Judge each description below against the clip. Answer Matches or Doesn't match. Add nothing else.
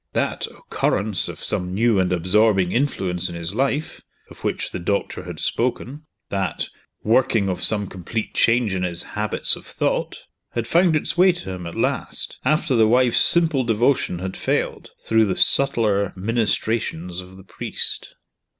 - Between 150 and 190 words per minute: Matches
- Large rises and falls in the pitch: Doesn't match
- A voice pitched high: Doesn't match